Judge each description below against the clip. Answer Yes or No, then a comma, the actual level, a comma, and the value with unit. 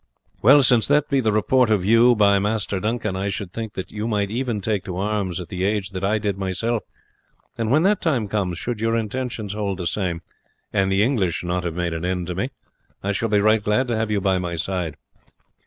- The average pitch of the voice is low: Yes, low, 105 Hz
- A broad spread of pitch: No, average, 3.4 semitones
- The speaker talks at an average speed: No, fast, 225 wpm